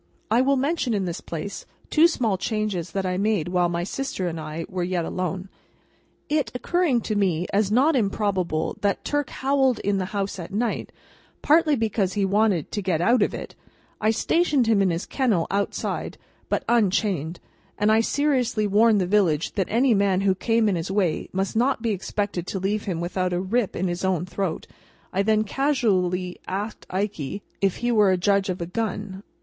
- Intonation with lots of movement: No, average, 3.7 semitones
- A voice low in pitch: No, high, 200 Hz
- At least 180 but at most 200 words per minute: Yes, average, 190 wpm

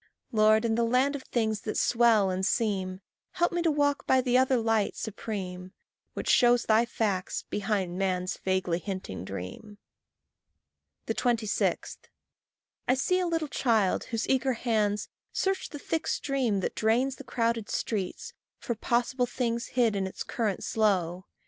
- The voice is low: No, high, 225 Hz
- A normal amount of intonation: Yes, average, 4.3 semitones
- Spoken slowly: No, average, 150 wpm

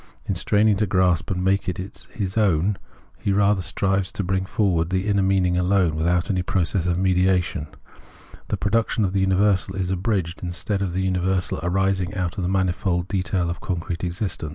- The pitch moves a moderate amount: No, narrow, 1.7 semitones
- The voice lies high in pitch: No, very low, 95 Hz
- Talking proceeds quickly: No, average, 185 wpm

